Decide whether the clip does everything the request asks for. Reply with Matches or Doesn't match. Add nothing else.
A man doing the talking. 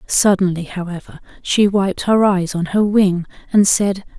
Doesn't match